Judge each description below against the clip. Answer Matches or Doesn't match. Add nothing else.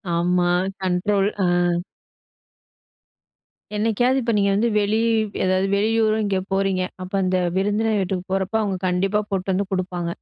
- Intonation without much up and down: Matches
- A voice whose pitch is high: Matches